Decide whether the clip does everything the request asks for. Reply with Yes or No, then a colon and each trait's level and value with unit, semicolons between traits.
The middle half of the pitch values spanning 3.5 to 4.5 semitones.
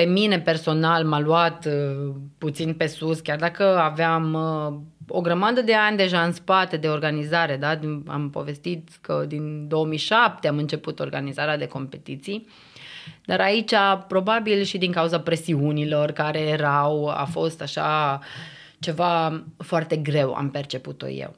No: narrow, 2.4 semitones